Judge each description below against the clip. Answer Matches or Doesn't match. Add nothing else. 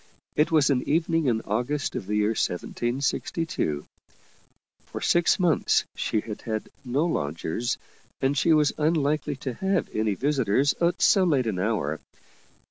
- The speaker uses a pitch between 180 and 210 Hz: Doesn't match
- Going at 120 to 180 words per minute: Matches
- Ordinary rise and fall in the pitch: Doesn't match